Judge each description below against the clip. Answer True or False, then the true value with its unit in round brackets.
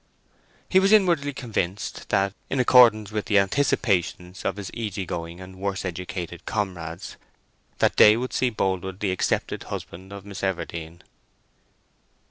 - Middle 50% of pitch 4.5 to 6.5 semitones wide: False (3.5 semitones)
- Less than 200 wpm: True (140 wpm)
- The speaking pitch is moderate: False (100 Hz)